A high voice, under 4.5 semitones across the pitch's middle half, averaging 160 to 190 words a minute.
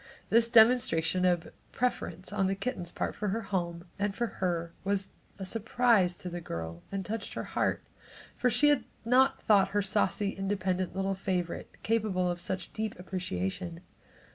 Yes: high, 195 Hz; average, 3.5 semitones; average, 165 wpm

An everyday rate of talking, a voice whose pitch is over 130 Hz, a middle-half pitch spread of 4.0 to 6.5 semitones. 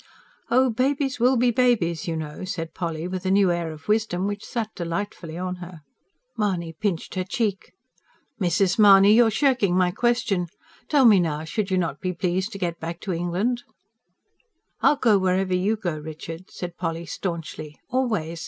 Yes: average, 170 wpm; medium, 185 Hz; average, 4.3 semitones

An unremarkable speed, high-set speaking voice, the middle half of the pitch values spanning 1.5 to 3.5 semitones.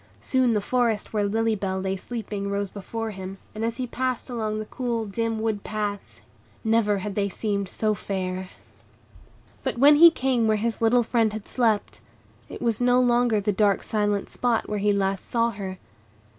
Yes: average, 185 wpm; high, 215 Hz; narrow, 2.6 semitones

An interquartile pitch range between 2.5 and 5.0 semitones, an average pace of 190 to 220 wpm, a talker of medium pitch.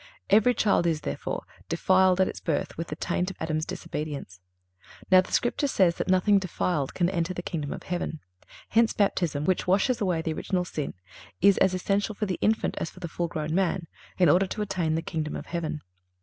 Yes: average, 3.2 semitones; average, 200 wpm; medium, 180 Hz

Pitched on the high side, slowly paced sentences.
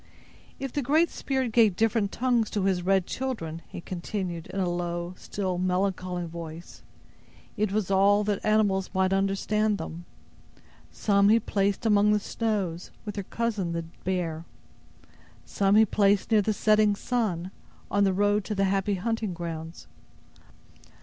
No: high, 195 Hz; average, 150 wpm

